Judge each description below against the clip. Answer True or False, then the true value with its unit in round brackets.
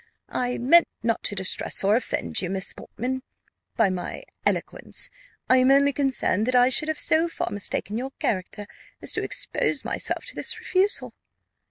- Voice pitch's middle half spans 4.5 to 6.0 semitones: True (5.3 semitones)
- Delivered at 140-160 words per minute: False (170 wpm)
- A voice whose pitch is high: True (245 Hz)